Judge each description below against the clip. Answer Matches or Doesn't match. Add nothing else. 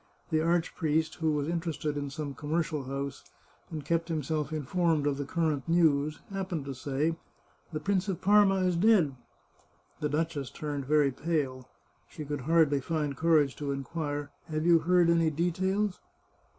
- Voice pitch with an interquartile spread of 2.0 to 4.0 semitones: Matches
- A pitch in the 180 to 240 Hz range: Doesn't match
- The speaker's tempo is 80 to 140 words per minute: Doesn't match